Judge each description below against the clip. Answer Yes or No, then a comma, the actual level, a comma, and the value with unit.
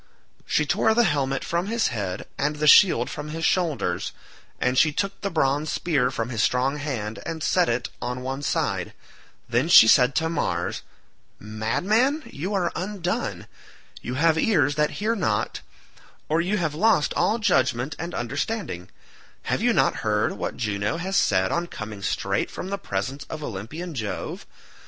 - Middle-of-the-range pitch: Yes, medium, 150 Hz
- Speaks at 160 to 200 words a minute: Yes, average, 165 wpm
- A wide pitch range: Yes, wide, 6.8 semitones